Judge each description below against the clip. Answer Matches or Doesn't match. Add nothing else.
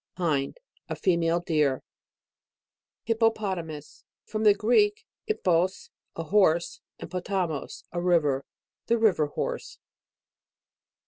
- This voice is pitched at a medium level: Matches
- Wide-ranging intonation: Doesn't match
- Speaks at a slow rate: Matches